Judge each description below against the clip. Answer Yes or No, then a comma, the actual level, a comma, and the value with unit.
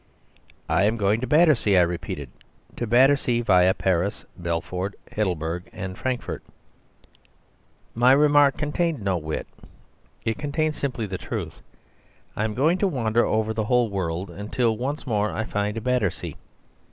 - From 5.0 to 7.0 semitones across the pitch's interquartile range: Yes, wide, 5.4 semitones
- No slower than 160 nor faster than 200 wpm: No, average, 140 wpm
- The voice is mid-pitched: No, low, 110 Hz